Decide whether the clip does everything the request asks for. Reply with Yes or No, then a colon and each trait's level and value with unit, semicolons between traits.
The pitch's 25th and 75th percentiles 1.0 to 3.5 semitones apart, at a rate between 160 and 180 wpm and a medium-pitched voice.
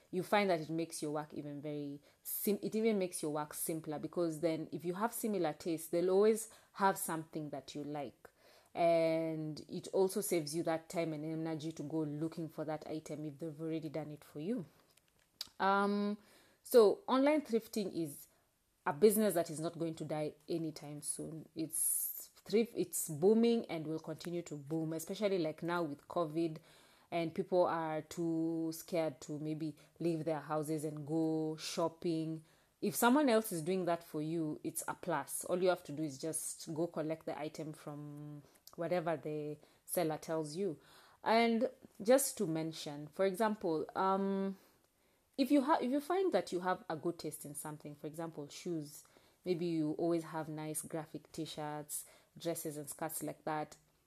Yes: average, 2.9 semitones; average, 175 wpm; medium, 165 Hz